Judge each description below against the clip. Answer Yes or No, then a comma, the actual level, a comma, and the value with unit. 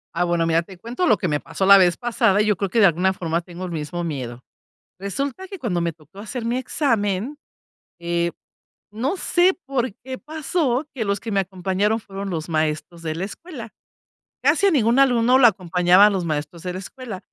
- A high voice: Yes, high, 195 Hz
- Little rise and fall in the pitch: No, wide, 5.9 semitones